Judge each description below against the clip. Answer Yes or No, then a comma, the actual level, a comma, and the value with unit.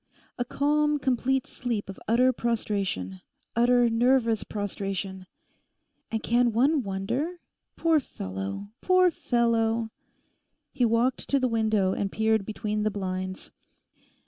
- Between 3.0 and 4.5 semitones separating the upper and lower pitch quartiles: Yes, average, 4.0 semitones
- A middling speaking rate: No, slow, 115 wpm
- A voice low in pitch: No, high, 225 Hz